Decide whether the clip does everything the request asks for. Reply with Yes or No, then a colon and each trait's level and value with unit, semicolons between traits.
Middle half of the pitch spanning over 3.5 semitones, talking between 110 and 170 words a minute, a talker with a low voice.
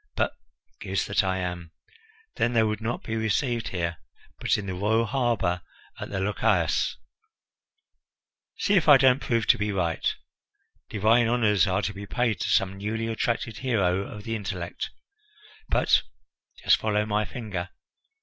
No: average, 3.2 semitones; average, 155 wpm; low, 105 Hz